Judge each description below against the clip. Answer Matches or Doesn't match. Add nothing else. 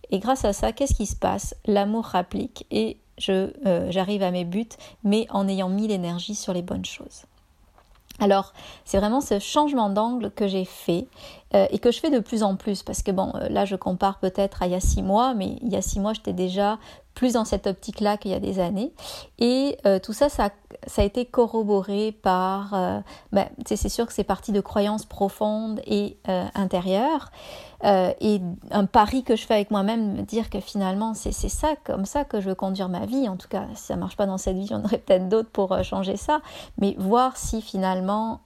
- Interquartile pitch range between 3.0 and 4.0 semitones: Doesn't match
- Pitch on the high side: Matches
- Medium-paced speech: Doesn't match